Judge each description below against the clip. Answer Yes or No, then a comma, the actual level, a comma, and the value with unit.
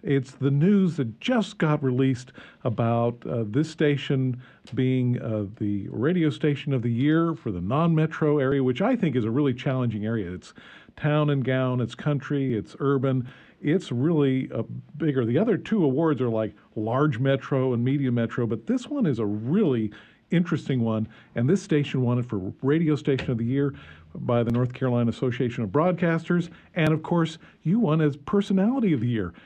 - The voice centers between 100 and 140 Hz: Yes, low, 135 Hz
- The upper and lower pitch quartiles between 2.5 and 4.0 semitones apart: No, average, 4.7 semitones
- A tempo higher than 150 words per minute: Yes, average, 185 wpm